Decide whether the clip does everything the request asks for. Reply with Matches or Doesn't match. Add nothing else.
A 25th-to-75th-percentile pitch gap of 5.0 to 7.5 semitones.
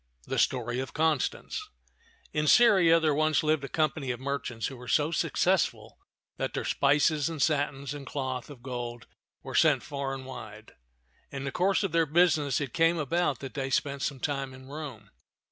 Doesn't match